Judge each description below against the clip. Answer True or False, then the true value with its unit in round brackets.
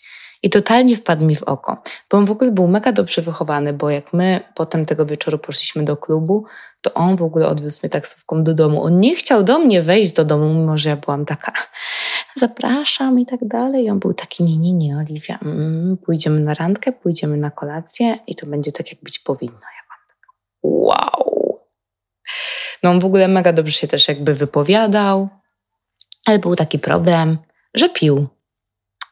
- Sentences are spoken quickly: True (190 wpm)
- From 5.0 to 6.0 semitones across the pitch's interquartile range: True (5.5 semitones)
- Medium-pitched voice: True (170 Hz)